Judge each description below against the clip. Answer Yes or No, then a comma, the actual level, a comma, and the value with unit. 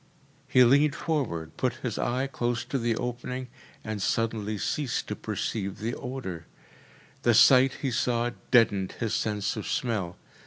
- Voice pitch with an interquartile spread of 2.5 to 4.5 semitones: Yes, average, 3.3 semitones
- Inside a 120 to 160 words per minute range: Yes, average, 150 wpm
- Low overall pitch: Yes, low, 120 Hz